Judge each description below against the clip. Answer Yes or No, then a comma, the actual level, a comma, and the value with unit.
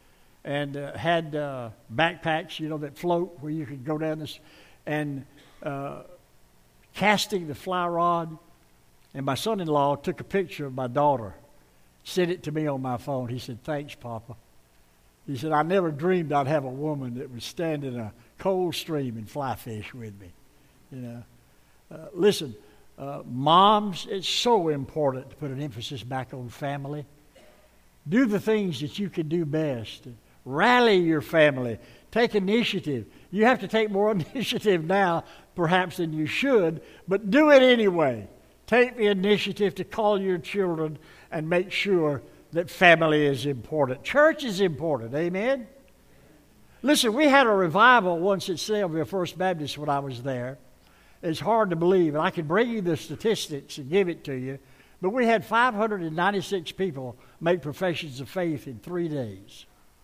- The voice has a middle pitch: Yes, medium, 155 Hz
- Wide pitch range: Yes, wide, 5.8 semitones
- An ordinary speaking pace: Yes, average, 170 wpm